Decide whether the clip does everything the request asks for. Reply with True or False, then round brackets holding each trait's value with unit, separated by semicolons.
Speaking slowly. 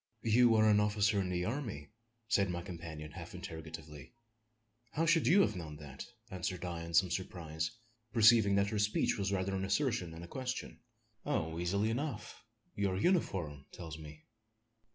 False (165 wpm)